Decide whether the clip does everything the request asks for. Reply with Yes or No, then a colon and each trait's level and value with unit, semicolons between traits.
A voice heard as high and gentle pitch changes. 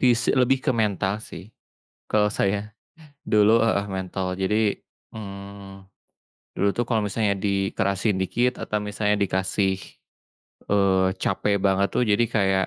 No: low, 100 Hz; narrow, 1.9 semitones